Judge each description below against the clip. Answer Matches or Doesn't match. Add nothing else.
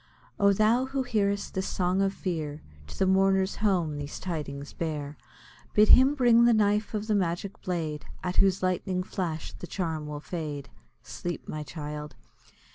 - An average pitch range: Matches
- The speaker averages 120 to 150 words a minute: Doesn't match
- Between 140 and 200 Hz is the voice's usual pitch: Matches